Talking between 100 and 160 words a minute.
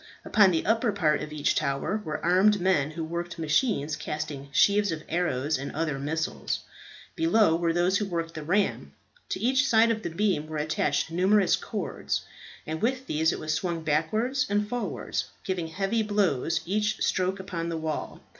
No: average, 175 wpm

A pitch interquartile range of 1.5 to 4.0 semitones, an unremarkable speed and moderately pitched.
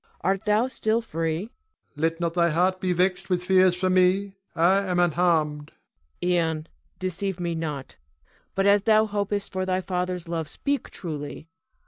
Yes: average, 2.7 semitones; average, 165 wpm; medium, 180 Hz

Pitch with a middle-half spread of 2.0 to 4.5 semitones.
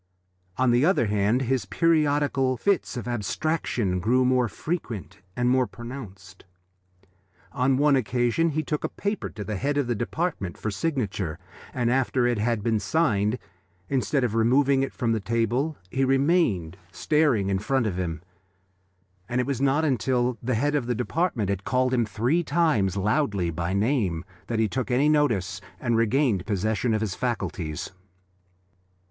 No: average, 4.9 semitones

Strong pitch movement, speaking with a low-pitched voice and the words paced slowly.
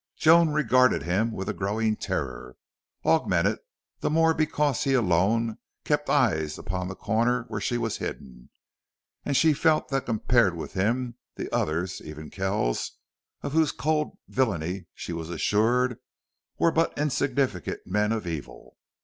No: wide, 6.8 semitones; low, 110 Hz; average, 145 wpm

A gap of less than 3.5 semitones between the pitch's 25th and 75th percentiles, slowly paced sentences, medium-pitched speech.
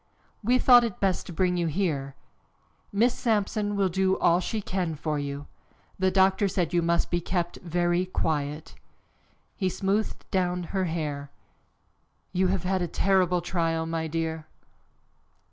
No: average, 2.8 semitones; average, 150 wpm; medium, 180 Hz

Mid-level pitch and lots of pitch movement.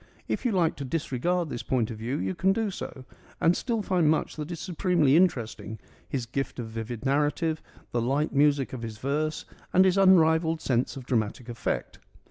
Yes: medium, 145 Hz; wide, 5.9 semitones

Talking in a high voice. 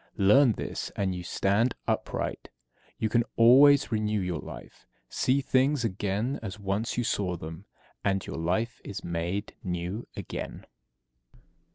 No: low, 105 Hz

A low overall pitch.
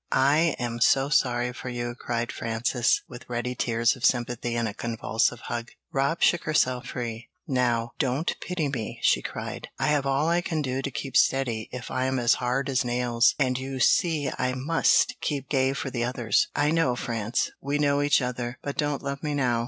Yes: low, 130 Hz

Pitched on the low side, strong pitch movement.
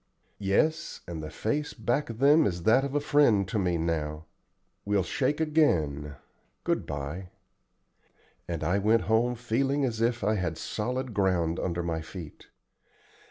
Yes: low, 105 Hz; wide, 7.3 semitones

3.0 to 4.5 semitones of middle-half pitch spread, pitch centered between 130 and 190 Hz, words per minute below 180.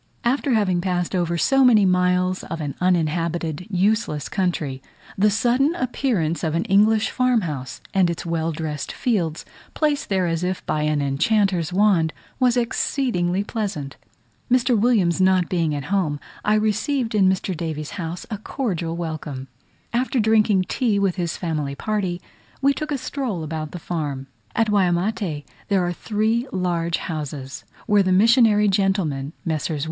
No: average, 4.9 semitones; medium, 185 Hz; average, 155 wpm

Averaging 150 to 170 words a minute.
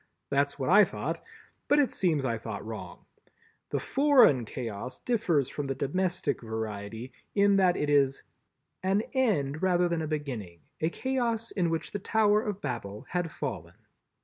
Yes: average, 160 wpm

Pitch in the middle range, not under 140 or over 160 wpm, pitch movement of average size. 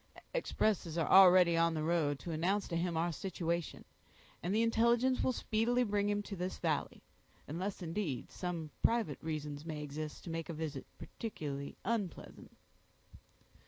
Yes: medium, 170 Hz; average, 155 wpm; average, 4.6 semitones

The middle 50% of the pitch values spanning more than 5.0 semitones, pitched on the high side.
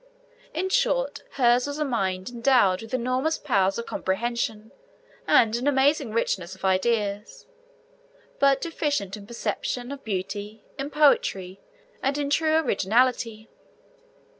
Yes: wide, 5.6 semitones; high, 235 Hz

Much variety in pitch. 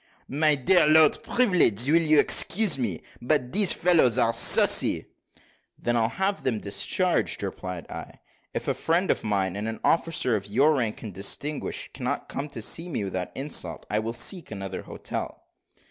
Yes: wide, 7.5 semitones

